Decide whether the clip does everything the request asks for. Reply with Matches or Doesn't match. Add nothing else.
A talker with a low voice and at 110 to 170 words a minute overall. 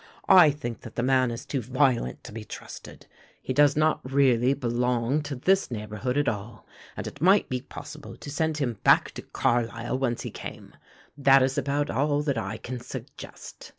Doesn't match